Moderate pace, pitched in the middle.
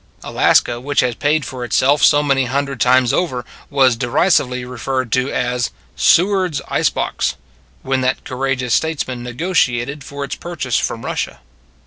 No: average, 160 wpm; low, 130 Hz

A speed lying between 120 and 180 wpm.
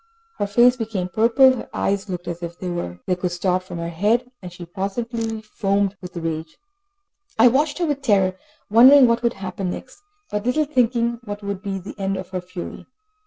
No: average, 190 wpm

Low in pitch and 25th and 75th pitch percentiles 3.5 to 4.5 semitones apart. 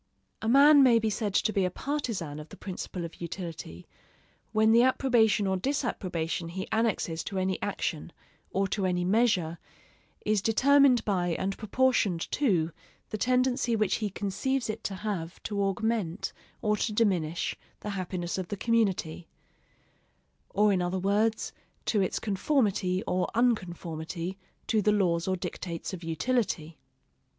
No: high, 195 Hz; average, 4.1 semitones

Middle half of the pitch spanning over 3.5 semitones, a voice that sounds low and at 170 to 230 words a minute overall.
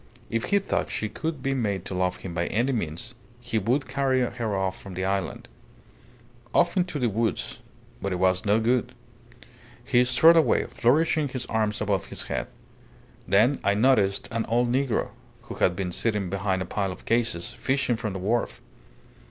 Yes: average, 4.8 semitones; low, 110 Hz; average, 180 wpm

